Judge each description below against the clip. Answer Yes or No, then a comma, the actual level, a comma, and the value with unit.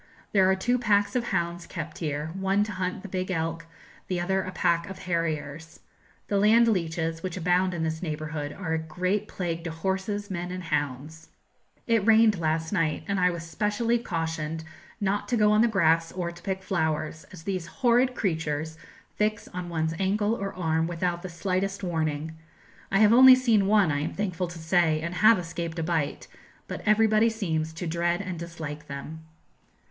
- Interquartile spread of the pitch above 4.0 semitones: No, average, 3.7 semitones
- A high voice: No, medium, 175 Hz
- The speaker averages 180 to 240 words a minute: Yes, average, 185 wpm